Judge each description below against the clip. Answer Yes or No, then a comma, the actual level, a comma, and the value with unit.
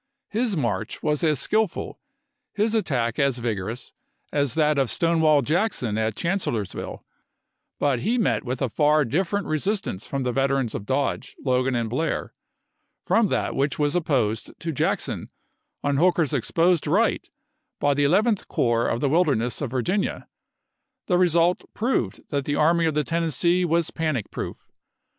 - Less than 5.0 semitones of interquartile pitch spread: No, average, 5.3 semitones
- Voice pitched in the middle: Yes, medium, 150 Hz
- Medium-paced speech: Yes, average, 150 wpm